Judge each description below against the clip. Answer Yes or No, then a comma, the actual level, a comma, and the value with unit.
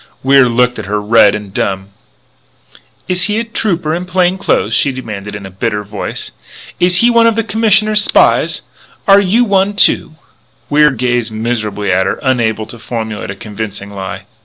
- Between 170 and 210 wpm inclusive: Yes, average, 175 wpm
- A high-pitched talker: No, low, 125 Hz